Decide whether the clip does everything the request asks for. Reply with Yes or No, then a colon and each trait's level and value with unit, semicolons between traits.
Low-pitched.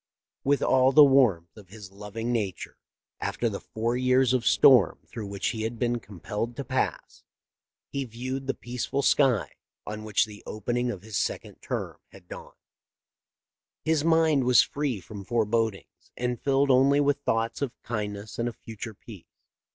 Yes: low, 120 Hz